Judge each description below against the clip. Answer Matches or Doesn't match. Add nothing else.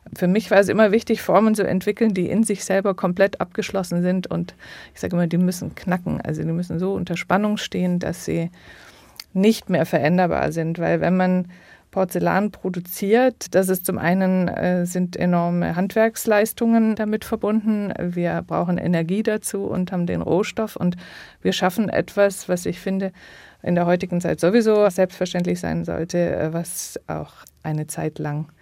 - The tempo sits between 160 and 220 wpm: Matches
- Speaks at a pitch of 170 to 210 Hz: Matches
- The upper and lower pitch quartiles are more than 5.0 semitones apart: Doesn't match